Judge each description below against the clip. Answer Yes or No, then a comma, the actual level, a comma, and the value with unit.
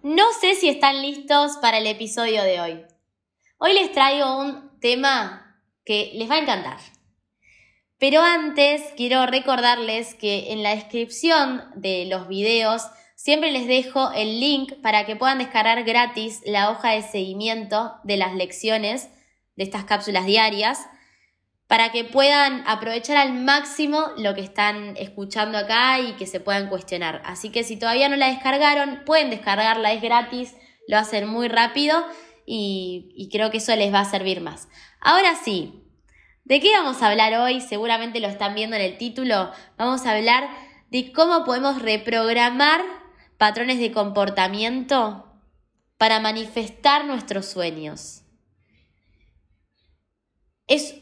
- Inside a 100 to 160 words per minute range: Yes, average, 145 wpm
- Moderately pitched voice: No, high, 225 Hz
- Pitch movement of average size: Yes, average, 4.6 semitones